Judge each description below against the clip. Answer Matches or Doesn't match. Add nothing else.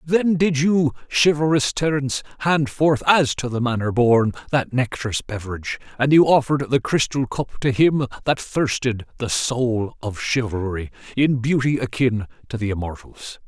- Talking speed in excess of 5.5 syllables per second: Doesn't match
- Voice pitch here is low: Matches